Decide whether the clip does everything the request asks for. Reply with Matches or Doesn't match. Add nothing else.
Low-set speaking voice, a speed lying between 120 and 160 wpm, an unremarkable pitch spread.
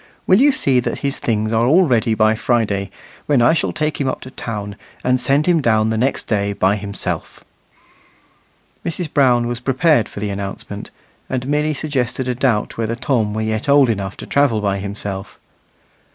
Doesn't match